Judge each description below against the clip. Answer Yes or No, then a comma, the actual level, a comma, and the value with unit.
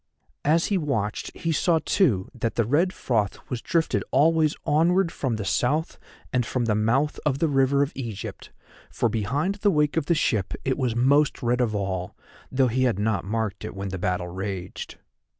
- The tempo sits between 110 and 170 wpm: No, average, 190 wpm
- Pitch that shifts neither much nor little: No, wide, 6.0 semitones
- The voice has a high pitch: No, low, 125 Hz